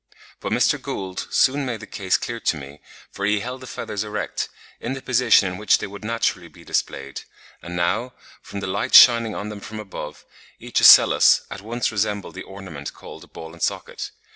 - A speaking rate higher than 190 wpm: Yes, average, 200 wpm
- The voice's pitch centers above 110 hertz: No, low, 105 Hz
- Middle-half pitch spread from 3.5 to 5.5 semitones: Yes, average, 3.8 semitones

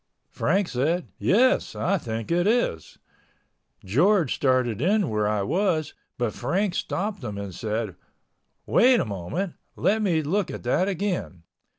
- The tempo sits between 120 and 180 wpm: Yes, average, 145 wpm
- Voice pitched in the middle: Yes, medium, 160 Hz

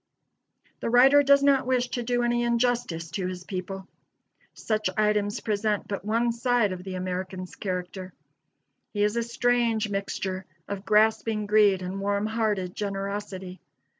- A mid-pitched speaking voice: No, high, 210 Hz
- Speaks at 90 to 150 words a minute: Yes, average, 145 wpm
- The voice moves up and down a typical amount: Yes, average, 3.7 semitones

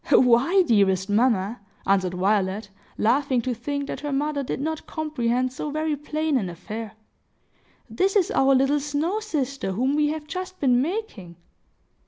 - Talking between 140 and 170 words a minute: Yes, average, 155 wpm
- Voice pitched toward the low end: No, very high, 270 Hz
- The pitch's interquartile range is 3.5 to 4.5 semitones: No, wide, 5.5 semitones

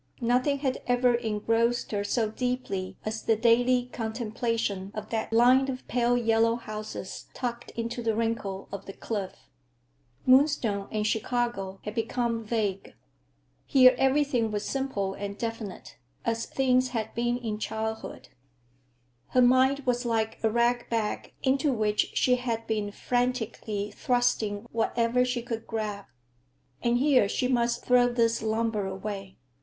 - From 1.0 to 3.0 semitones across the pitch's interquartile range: Yes, narrow, 2.5 semitones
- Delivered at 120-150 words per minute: Yes, average, 140 wpm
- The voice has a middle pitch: No, high, 230 Hz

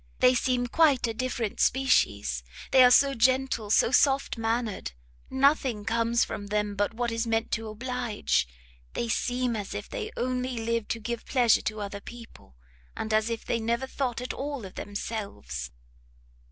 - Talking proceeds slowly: No, average, 165 wpm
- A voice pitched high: Yes, high, 235 Hz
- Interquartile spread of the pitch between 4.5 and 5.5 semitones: No, average, 2.8 semitones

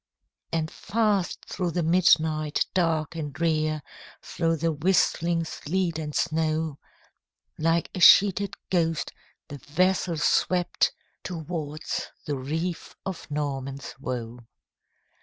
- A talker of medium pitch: Yes, medium, 160 Hz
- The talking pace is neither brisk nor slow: No, slow, 105 wpm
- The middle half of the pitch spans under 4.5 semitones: Yes, narrow, 2.6 semitones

